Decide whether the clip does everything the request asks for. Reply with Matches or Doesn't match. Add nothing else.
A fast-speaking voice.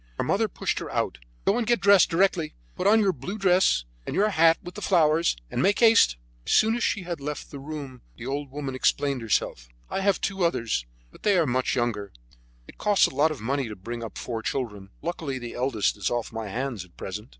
Matches